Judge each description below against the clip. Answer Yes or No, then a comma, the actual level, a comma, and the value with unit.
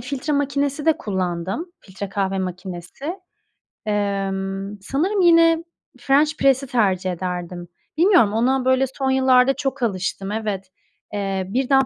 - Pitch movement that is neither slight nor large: No, wide, 6.1 semitones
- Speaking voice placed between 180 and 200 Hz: No, high, 225 Hz